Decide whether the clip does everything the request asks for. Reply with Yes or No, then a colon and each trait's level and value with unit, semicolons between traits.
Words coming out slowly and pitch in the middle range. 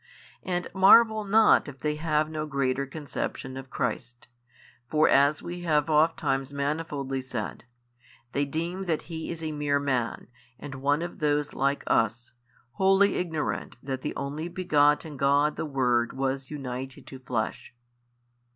No: average, 145 wpm; medium, 145 Hz